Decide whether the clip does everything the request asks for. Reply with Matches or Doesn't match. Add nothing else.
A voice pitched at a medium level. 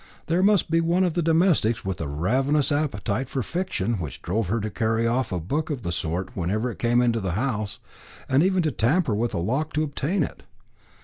Doesn't match